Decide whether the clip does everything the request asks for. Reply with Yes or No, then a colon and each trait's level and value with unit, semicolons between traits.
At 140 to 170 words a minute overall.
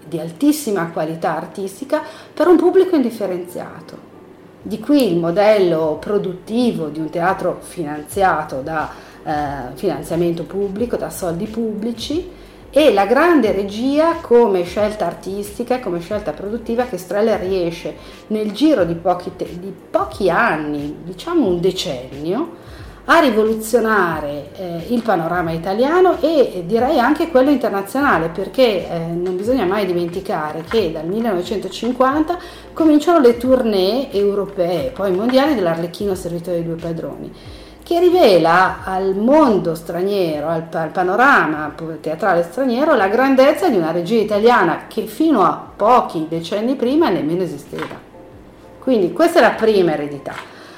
No: average, 130 wpm